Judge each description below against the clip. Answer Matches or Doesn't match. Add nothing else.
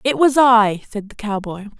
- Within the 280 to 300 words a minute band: Doesn't match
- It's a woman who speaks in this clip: Matches